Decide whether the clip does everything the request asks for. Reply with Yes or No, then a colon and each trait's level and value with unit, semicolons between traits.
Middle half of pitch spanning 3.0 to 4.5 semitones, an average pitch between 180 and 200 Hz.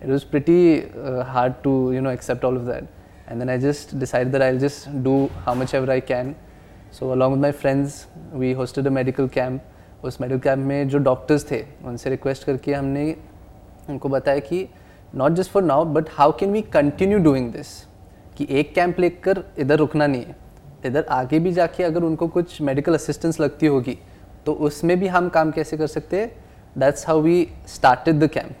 No: average, 3.4 semitones; medium, 140 Hz